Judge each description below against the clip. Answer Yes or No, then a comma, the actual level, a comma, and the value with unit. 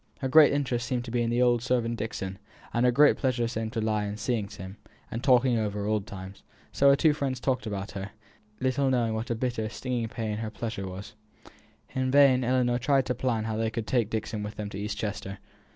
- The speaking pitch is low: Yes, low, 115 Hz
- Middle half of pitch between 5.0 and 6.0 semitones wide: No, average, 3.0 semitones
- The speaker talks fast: Yes, fast, 220 wpm